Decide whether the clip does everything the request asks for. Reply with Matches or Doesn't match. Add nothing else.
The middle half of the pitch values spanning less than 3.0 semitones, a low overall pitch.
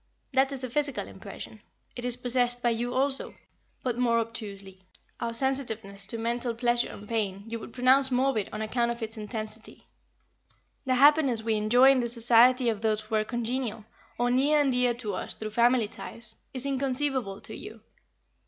Doesn't match